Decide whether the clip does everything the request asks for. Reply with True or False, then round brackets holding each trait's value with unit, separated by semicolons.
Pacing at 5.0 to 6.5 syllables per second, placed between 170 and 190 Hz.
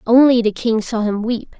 False (5.1 syllables/s; 230 Hz)